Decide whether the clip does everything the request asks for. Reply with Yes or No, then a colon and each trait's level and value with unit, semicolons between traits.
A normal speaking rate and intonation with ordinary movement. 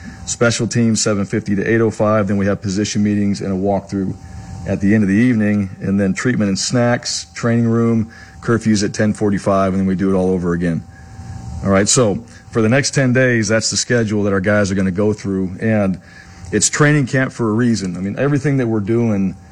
No: fast, 210 wpm; average, 3.0 semitones